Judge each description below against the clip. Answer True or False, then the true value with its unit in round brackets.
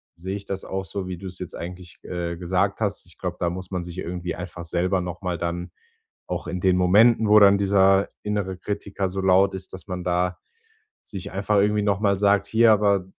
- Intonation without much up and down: True (2.0 semitones)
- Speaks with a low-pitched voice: True (95 Hz)